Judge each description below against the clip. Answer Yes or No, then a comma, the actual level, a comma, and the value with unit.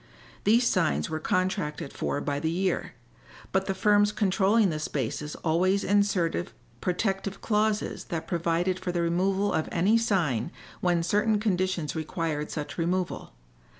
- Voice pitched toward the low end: No, medium, 185 Hz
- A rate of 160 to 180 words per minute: No, average, 140 wpm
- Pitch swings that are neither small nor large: Yes, average, 3.5 semitones